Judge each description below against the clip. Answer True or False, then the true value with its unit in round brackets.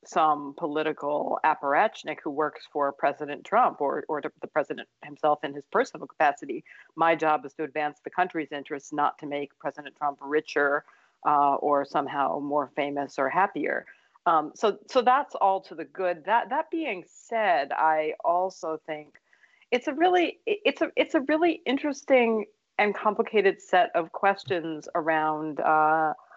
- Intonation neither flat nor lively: False (5.8 semitones)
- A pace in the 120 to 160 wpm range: True (155 wpm)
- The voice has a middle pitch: True (160 Hz)